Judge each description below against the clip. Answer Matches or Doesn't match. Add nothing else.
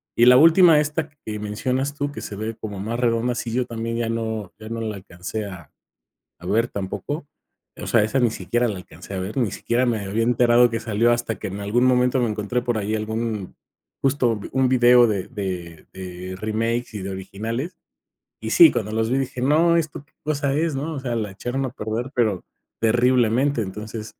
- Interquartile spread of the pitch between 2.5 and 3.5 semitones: Matches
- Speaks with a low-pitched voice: Matches